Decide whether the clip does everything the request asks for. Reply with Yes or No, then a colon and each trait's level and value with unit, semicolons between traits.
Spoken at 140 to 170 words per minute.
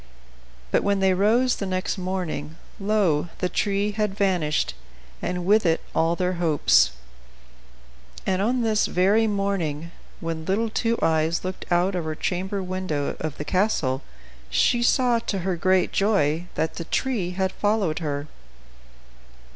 Yes: average, 145 wpm